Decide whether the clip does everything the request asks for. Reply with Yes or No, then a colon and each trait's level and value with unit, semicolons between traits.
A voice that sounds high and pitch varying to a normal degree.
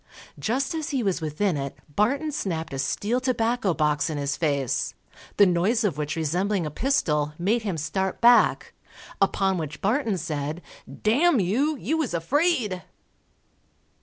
No: high, 195 Hz; wide, 7.6 semitones